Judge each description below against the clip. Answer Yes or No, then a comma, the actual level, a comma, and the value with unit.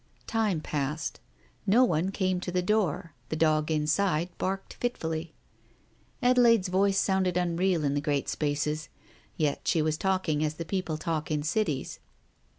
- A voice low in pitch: No, medium, 165 Hz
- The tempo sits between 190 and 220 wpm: No, average, 145 wpm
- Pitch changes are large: No, average, 3.8 semitones